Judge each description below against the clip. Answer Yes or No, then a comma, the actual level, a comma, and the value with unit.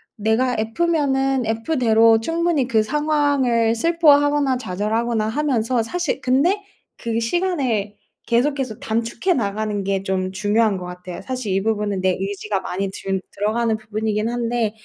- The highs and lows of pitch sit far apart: No, average, 4.3 semitones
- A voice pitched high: Yes, high, 230 Hz